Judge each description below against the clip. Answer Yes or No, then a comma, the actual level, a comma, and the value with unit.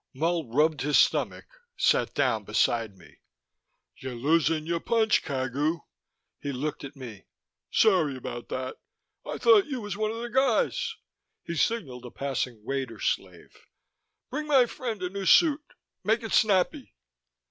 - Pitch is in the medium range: Yes, medium, 165 Hz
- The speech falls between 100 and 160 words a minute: Yes, average, 145 wpm